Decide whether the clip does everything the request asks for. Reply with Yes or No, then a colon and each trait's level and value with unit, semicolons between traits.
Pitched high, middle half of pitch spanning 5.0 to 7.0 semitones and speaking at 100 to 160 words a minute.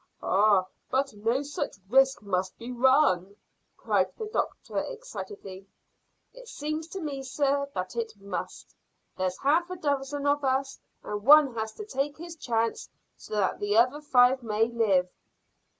Yes: very high, 260 Hz; wide, 5.5 semitones; average, 150 wpm